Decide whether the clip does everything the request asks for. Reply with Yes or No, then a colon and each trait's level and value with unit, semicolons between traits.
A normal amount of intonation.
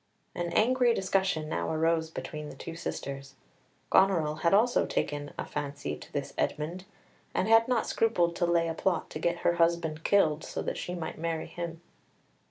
Yes: average, 3.5 semitones